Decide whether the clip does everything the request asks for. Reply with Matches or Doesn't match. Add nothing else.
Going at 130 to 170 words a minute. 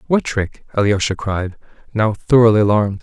Matches